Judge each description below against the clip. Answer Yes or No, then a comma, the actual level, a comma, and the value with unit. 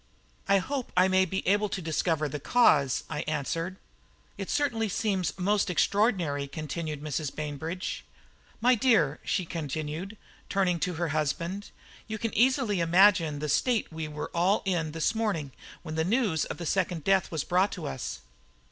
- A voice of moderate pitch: Yes, medium, 175 Hz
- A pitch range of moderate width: Yes, average, 4.6 semitones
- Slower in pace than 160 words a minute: No, average, 165 wpm